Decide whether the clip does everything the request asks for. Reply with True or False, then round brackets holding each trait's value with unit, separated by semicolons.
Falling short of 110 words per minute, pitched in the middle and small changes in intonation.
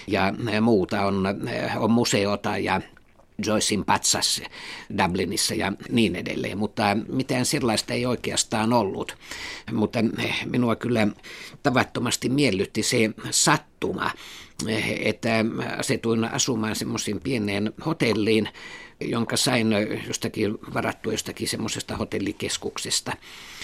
False (95 wpm; 110 Hz; 1.8 semitones)